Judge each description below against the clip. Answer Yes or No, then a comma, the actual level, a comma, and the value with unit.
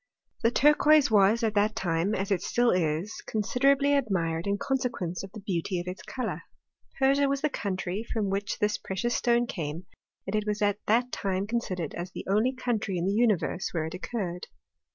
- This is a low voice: No, high, 205 Hz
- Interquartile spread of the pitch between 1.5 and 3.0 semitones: No, average, 4.6 semitones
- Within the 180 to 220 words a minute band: Yes, average, 195 wpm